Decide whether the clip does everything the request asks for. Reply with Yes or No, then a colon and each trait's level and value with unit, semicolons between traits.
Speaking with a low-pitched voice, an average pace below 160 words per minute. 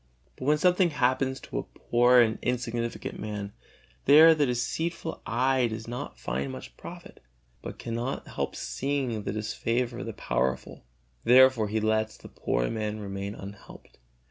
Yes: low, 120 Hz; average, 150 wpm